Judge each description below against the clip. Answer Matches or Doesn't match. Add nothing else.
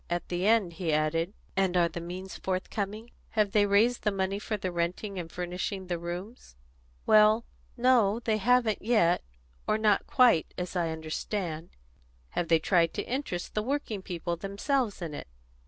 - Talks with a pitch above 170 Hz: Matches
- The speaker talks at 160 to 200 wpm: Matches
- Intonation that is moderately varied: Matches